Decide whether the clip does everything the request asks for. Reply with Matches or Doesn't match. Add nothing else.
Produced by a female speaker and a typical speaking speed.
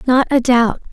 Matches